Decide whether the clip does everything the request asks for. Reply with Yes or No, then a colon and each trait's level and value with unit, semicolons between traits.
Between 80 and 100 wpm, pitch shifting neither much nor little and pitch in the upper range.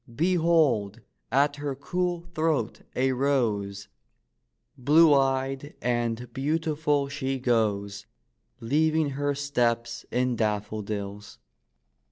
No: slow, 90 wpm; average, 4.1 semitones; low, 135 Hz